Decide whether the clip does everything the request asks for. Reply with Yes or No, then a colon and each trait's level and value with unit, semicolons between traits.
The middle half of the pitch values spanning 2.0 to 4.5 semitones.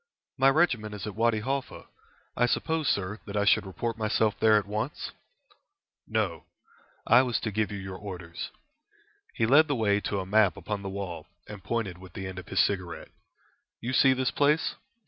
Yes: average, 3.9 semitones